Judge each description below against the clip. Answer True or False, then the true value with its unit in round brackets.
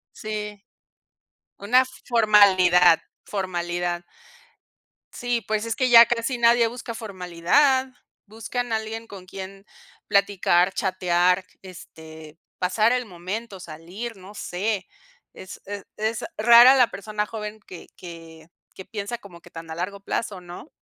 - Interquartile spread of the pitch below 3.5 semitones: False (4.1 semitones)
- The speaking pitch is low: False (200 Hz)